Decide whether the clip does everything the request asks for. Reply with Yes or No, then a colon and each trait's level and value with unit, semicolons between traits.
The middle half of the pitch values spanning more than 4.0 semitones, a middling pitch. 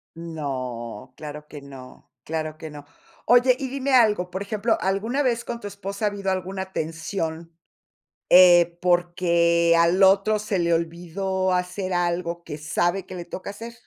No: average, 3.2 semitones; medium, 180 Hz